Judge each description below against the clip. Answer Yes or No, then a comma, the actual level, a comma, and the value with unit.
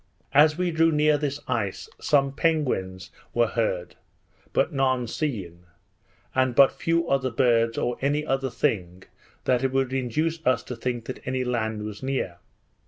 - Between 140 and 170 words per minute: Yes, average, 150 wpm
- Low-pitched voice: Yes, low, 130 Hz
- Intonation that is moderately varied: Yes, average, 4.0 semitones